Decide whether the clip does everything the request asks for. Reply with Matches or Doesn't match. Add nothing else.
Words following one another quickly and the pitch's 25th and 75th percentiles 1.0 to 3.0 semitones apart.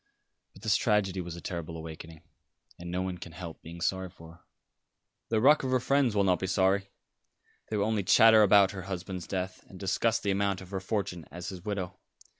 Matches